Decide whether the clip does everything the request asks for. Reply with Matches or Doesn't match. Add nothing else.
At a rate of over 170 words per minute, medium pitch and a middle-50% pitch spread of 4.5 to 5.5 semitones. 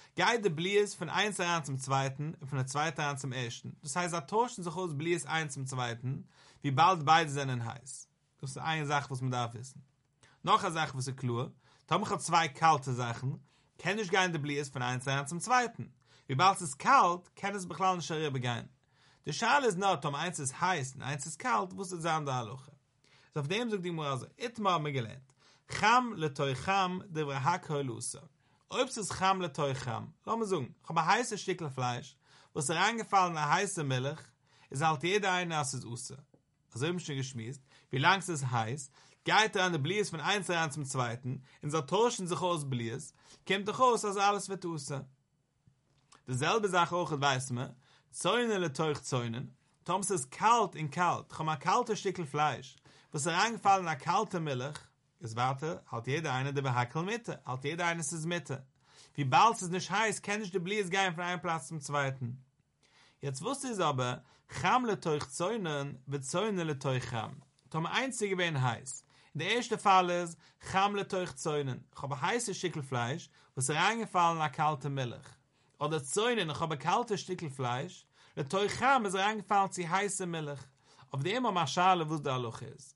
Matches